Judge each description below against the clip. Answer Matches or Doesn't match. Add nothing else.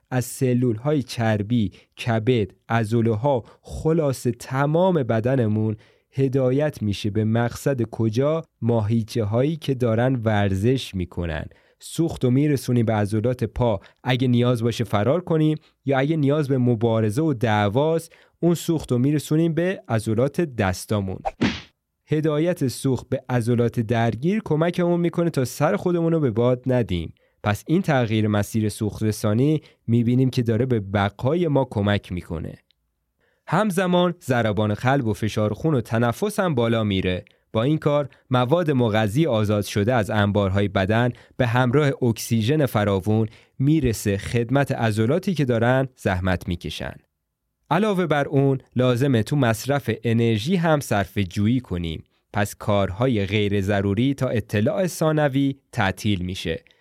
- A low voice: Matches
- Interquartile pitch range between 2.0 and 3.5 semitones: Doesn't match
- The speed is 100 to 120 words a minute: Doesn't match